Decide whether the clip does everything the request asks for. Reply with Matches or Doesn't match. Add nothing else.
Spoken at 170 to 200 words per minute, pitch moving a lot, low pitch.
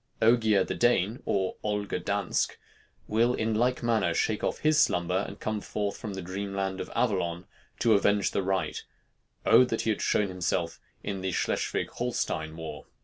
Doesn't match